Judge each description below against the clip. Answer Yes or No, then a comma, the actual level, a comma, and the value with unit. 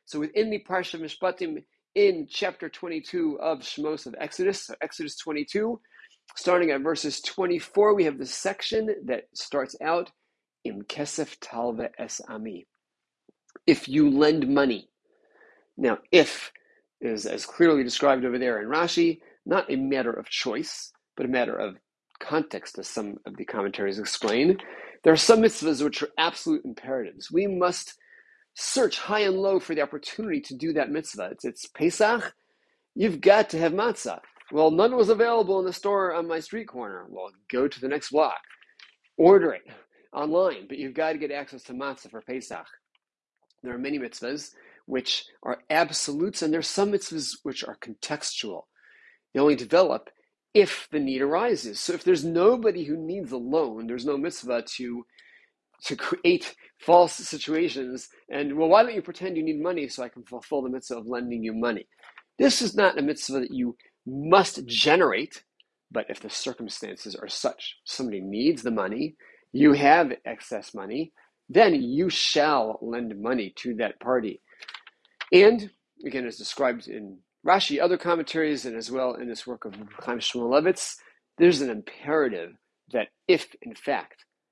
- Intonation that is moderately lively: No, wide, 8.6 semitones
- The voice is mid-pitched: Yes, medium, 170 Hz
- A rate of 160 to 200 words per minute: Yes, average, 165 wpm